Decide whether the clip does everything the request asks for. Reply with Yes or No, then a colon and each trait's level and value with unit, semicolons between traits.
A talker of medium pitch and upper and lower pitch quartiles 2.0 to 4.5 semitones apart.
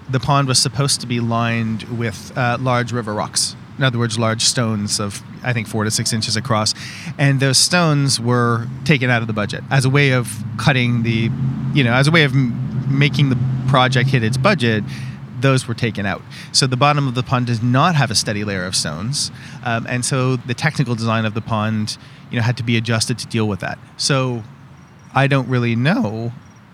No: low, 125 Hz; average, 2.9 semitones